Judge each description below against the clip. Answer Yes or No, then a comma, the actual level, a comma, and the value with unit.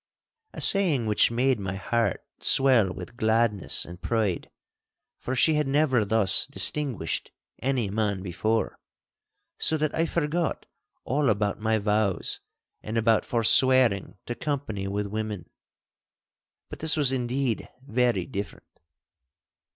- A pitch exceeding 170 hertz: No, low, 115 Hz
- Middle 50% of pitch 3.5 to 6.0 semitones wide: Yes, average, 4.6 semitones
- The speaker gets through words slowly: Yes, slow, 125 wpm